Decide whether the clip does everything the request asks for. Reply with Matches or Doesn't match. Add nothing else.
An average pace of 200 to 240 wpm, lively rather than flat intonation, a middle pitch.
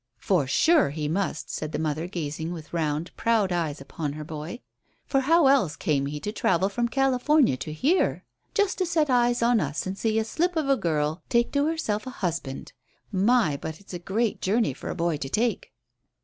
Doesn't match